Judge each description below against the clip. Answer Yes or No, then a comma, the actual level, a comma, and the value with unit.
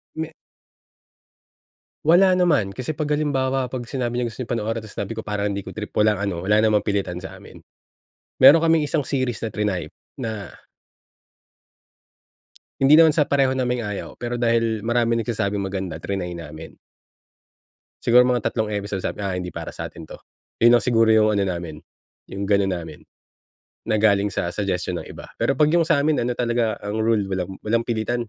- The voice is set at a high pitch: No, low, 110 Hz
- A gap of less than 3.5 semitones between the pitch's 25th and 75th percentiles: No, average, 4.1 semitones